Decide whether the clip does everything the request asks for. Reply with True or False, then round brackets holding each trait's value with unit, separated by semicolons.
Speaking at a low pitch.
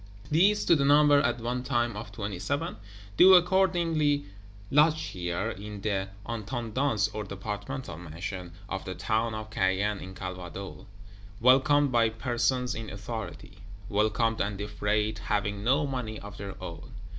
True (110 Hz)